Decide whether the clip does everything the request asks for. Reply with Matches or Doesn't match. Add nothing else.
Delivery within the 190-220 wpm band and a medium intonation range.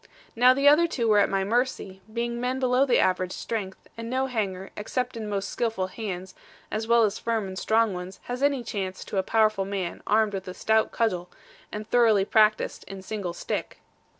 Matches